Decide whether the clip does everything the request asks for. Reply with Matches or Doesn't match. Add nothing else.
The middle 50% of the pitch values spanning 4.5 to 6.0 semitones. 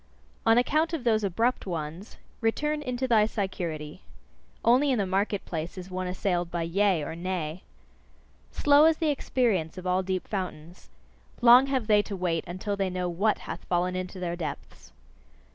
Matches